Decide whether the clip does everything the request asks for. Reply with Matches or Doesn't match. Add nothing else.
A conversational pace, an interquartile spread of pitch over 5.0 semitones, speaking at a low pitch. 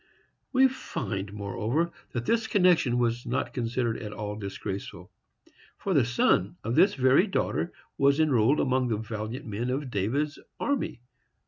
Matches